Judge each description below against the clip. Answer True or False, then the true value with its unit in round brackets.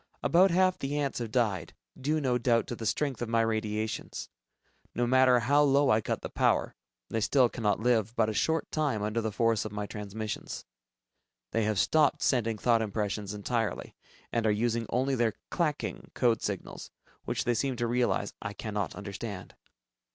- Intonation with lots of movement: False (3.3 semitones)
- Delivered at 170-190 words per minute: True (180 wpm)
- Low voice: True (115 Hz)